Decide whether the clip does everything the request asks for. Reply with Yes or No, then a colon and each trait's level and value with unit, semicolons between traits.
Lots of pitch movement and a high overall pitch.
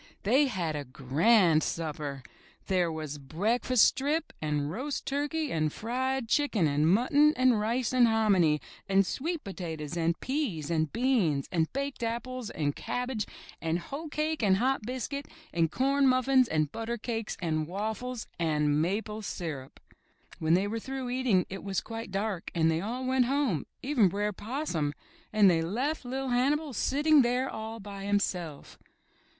Yes: wide, 7.7 semitones; high, 215 Hz